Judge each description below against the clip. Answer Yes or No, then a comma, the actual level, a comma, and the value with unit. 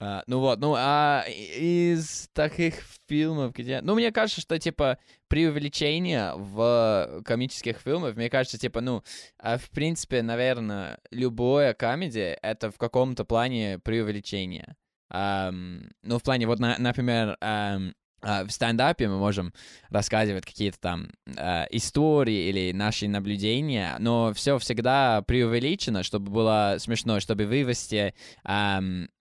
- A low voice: Yes, low, 115 Hz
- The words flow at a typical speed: Yes, average, 135 wpm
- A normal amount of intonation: Yes, average, 4.6 semitones